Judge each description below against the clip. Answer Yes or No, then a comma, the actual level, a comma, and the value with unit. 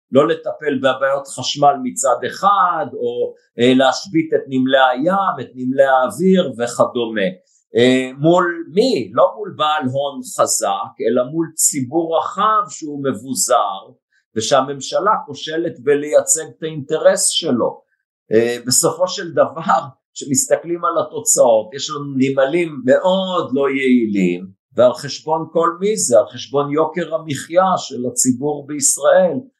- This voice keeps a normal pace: Yes, average, 125 wpm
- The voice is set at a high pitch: No, medium, 150 Hz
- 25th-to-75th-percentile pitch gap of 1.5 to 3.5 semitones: No, wide, 5.5 semitones